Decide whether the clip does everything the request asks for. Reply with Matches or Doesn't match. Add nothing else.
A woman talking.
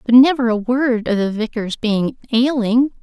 Matches